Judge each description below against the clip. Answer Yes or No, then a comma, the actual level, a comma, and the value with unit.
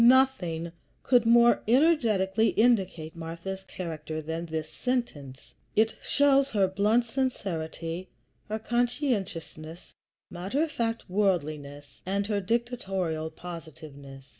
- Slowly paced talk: Yes, slow, 105 wpm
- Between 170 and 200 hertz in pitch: Yes, high, 190 Hz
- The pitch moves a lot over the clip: Yes, wide, 6.6 semitones